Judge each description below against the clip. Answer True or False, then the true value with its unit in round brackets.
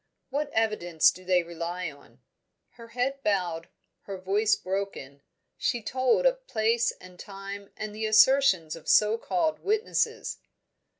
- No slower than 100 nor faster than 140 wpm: True (135 wpm)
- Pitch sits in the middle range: False (210 Hz)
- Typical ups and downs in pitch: True (5.0 semitones)